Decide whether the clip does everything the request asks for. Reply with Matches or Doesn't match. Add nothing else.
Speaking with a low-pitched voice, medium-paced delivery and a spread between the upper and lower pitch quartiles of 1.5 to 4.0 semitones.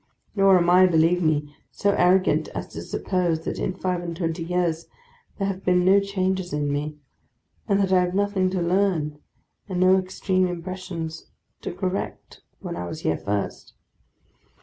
Doesn't match